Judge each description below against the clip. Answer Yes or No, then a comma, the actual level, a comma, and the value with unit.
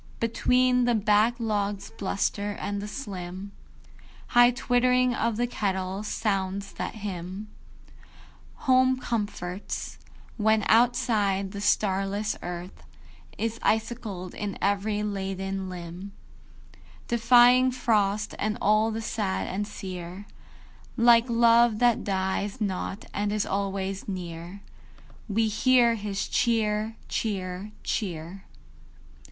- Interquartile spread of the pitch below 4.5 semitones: Yes, average, 3.1 semitones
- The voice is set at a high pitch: Yes, high, 205 Hz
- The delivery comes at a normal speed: No, slow, 105 wpm